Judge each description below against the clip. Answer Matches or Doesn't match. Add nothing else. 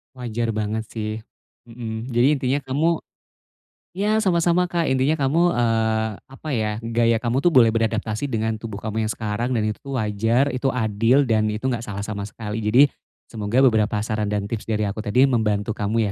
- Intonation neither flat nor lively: Matches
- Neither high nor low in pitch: Doesn't match